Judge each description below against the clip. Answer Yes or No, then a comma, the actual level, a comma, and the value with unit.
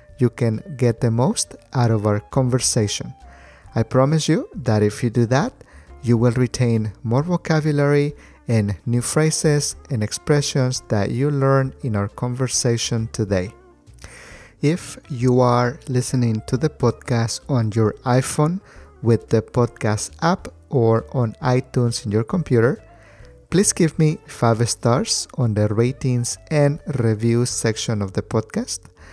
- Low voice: Yes, low, 120 Hz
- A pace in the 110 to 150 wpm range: Yes, average, 140 wpm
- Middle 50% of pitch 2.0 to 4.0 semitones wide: Yes, average, 3.5 semitones